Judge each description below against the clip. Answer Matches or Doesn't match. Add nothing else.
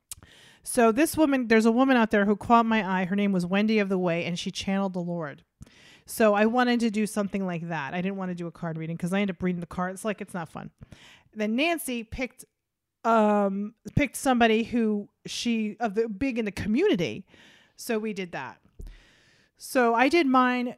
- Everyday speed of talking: Doesn't match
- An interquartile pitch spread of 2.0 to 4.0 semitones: Matches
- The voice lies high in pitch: Matches